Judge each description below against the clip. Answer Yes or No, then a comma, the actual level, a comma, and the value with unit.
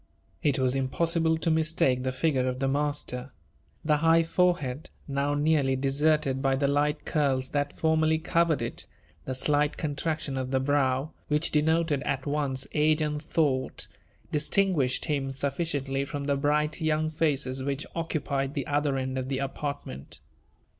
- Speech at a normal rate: Yes, average, 155 wpm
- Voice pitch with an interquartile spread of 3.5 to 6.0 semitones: No, narrow, 2.6 semitones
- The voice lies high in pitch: No, medium, 145 Hz